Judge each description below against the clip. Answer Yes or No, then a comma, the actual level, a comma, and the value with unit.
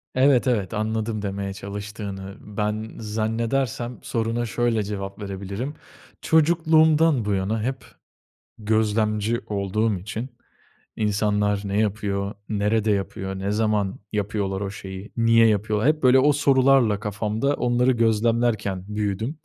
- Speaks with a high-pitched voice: No, low, 110 Hz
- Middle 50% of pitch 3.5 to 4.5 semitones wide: No, average, 2.7 semitones